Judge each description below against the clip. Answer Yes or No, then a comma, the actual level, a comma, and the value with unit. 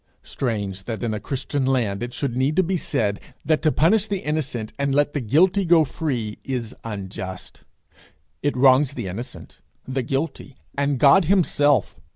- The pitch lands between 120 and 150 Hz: Yes, low, 135 Hz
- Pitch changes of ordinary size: Yes, average, 4.9 semitones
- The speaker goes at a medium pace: Yes, average, 170 wpm